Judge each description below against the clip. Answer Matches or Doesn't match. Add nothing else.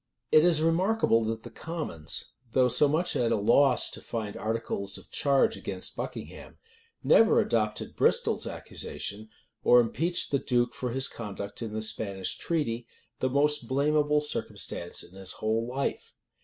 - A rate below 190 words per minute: Matches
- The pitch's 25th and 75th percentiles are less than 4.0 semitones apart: Doesn't match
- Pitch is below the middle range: Matches